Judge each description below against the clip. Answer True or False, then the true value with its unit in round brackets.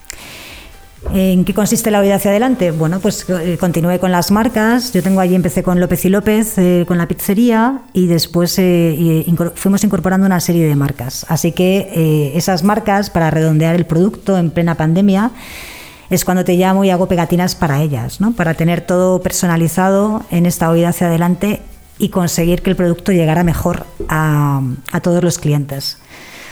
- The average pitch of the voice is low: False (180 Hz)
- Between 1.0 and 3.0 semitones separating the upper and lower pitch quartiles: True (2.5 semitones)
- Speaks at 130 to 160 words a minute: False (175 wpm)